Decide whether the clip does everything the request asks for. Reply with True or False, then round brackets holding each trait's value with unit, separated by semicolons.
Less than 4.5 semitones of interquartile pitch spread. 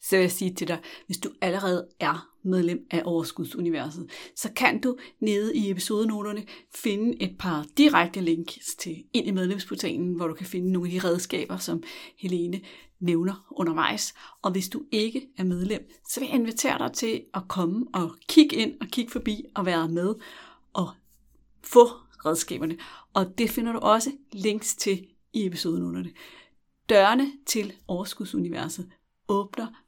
False (4.9 semitones)